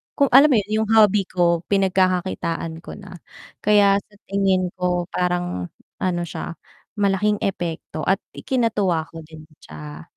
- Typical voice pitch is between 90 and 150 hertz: No, medium, 185 Hz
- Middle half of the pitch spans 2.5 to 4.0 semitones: Yes, average, 3.1 semitones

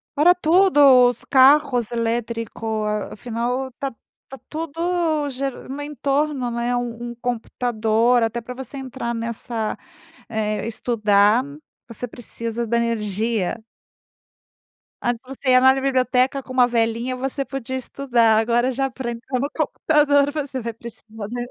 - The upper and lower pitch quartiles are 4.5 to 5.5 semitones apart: No, average, 2.8 semitones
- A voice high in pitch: Yes, high, 245 Hz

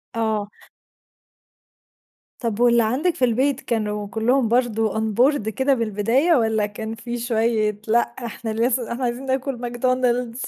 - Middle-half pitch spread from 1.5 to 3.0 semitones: Yes, narrow, 2.4 semitones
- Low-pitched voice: No, high, 235 Hz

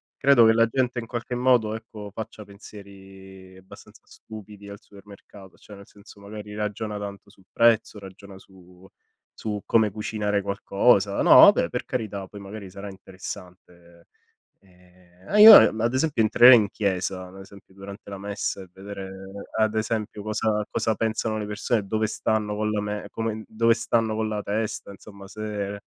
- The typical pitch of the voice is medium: No, low, 105 Hz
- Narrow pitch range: Yes, narrow, 1.9 semitones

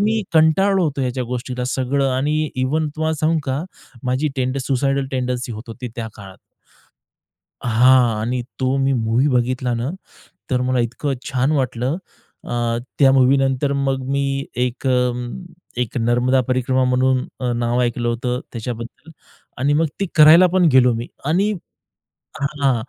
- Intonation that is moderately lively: No, narrow, 2.2 semitones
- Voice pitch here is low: Yes, low, 130 Hz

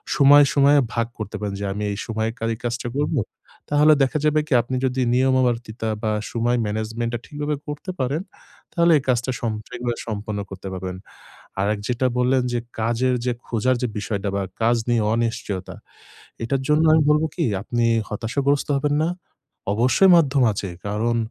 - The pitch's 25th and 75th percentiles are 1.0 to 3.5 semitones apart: No, average, 4.1 semitones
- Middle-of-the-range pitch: No, low, 120 Hz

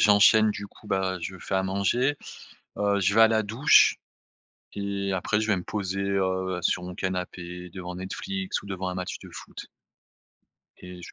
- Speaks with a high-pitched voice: No, very low, 95 Hz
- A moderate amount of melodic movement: No, narrow, 1.9 semitones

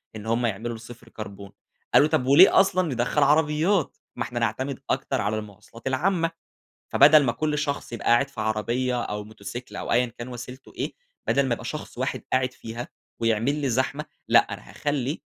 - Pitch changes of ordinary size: Yes, average, 4.0 semitones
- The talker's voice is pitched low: Yes, low, 125 Hz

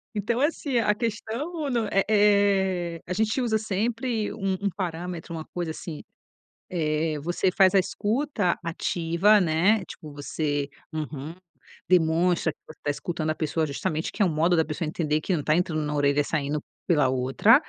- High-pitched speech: No, medium, 175 Hz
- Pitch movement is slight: No, average, 4.9 semitones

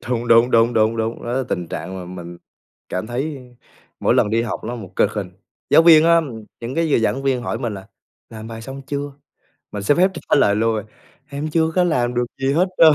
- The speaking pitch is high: No, low, 120 Hz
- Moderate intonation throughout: Yes, average, 4.6 semitones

